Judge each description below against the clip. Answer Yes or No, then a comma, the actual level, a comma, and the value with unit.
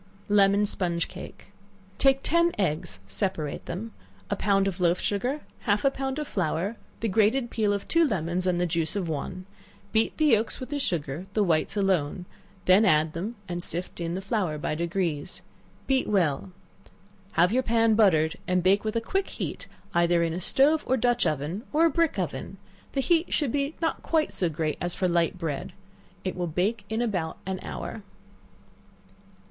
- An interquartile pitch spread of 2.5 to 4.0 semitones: No, average, 5.0 semitones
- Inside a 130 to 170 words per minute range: No, average, 185 wpm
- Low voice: No, high, 195 Hz